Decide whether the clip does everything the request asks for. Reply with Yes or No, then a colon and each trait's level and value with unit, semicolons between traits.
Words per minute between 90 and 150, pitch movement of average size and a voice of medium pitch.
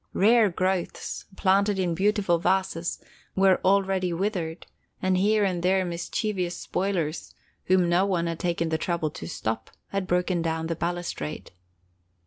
No: average, 140 wpm; narrow, 2.2 semitones; medium, 180 Hz